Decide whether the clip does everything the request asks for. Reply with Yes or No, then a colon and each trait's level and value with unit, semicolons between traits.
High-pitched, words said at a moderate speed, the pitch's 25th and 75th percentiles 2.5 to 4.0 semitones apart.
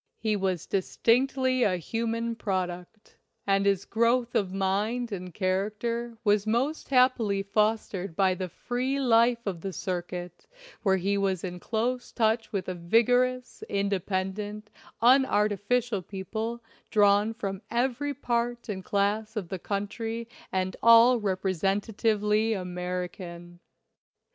No: high, 210 Hz; slow, 125 wpm; average, 3.6 semitones